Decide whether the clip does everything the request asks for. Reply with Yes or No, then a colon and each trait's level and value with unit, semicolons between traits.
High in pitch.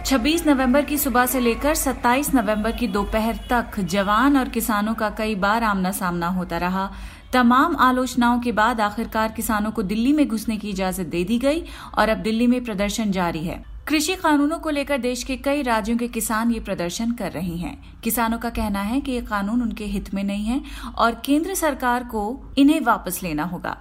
Yes: high, 230 Hz